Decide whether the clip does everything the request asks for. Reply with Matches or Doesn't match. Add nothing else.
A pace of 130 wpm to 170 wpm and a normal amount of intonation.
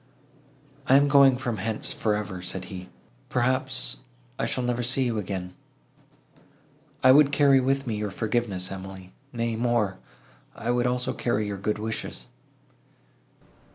Matches